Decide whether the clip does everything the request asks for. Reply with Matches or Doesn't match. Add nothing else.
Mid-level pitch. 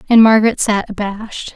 Doesn't match